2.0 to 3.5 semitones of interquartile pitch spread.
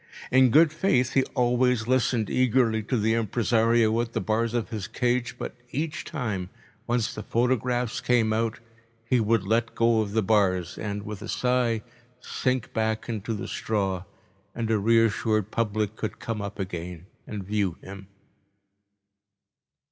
Yes: narrow, 2.5 semitones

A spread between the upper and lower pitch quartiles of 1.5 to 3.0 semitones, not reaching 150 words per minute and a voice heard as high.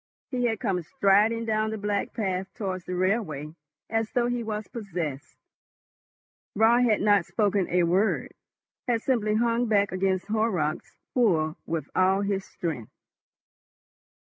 No: average, 3.4 semitones; average, 140 wpm; high, 205 Hz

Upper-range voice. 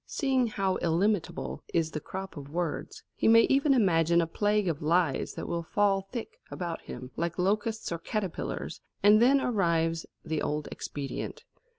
No: medium, 180 Hz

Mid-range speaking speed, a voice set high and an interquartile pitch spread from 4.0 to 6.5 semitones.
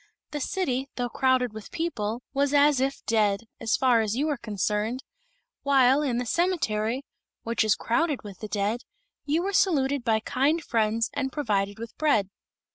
Yes: average, 170 wpm; very high, 250 Hz; average, 4.5 semitones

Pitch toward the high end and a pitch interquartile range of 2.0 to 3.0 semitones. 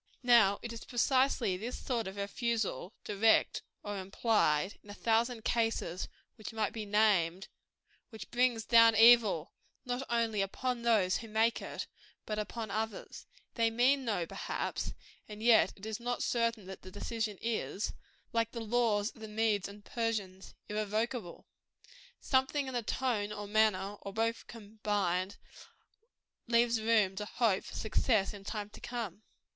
Yes: high, 220 Hz; narrow, 2.4 semitones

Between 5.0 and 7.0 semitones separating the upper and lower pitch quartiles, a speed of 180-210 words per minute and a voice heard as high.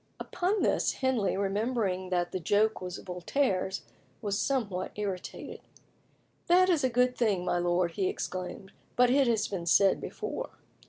No: wide, 5.4 semitones; average, 150 wpm; high, 200 Hz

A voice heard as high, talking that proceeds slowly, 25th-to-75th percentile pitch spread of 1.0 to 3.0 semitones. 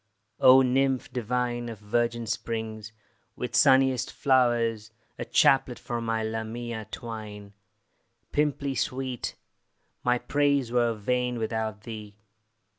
No: low, 120 Hz; slow, 110 wpm; narrow, 2.4 semitones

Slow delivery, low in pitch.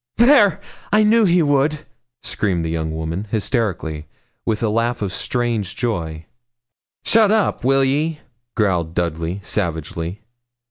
Yes: slow, 130 wpm; low, 110 Hz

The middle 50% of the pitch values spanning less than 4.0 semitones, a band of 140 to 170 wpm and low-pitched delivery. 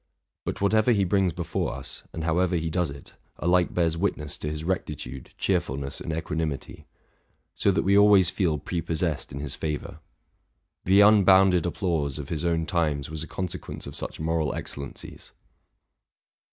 Yes: average, 3.4 semitones; average, 160 wpm; very low, 85 Hz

